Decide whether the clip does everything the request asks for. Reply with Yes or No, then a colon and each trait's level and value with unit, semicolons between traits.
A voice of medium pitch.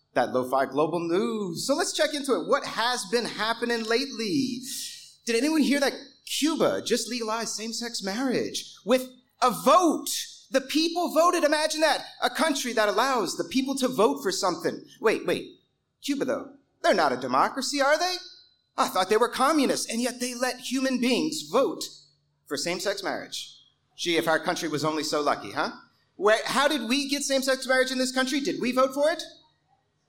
No: very high, 255 Hz